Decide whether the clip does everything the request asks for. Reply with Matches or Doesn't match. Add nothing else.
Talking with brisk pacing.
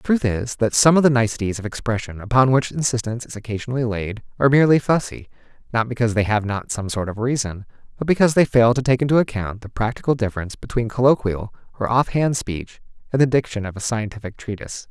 Matches